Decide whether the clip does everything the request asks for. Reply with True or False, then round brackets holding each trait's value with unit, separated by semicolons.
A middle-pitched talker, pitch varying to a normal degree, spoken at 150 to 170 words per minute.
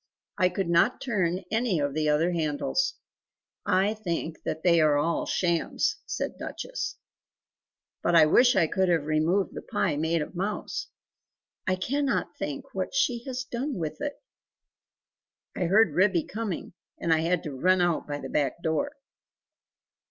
True (175 Hz; 4.7 semitones; 160 wpm)